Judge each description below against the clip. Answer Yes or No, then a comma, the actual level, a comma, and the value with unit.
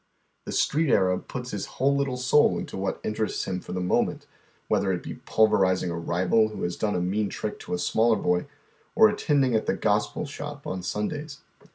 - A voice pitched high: No, low, 105 Hz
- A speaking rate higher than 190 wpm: Yes, average, 200 wpm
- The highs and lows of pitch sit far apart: Yes, wide, 6.5 semitones